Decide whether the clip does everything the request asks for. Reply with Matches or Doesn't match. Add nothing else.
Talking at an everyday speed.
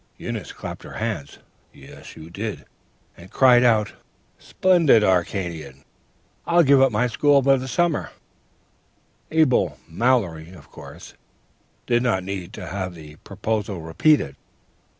Doesn't match